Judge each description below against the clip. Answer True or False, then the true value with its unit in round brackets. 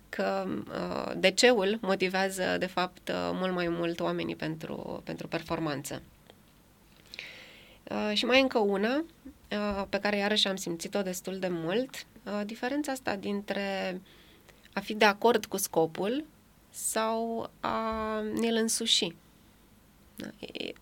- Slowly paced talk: True (130 wpm)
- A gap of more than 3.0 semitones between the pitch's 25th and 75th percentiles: True (3.5 semitones)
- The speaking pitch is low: False (200 Hz)